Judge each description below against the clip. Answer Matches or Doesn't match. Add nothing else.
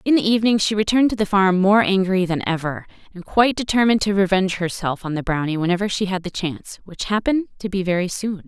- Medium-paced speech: Doesn't match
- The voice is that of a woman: Matches